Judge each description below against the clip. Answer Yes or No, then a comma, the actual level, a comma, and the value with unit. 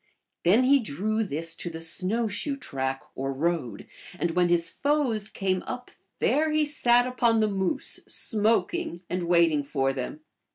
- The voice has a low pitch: No, high, 190 Hz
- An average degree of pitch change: No, wide, 6.5 semitones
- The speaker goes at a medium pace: Yes, average, 165 wpm